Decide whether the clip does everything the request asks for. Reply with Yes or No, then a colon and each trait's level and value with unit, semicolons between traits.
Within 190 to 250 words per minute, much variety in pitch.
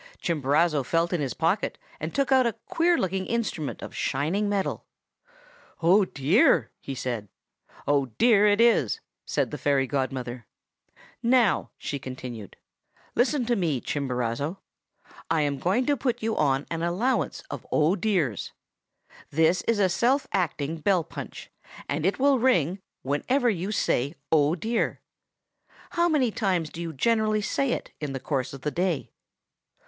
No: average, 155 wpm; wide, 7.7 semitones